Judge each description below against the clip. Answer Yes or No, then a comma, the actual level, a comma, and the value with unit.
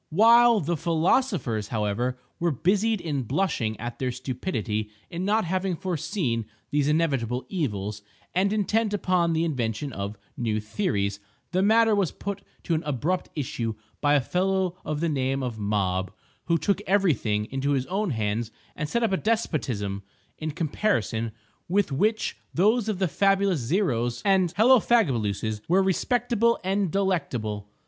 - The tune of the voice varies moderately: No, wide, 8.7 semitones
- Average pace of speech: Yes, average, 150 wpm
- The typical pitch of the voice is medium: Yes, medium, 160 Hz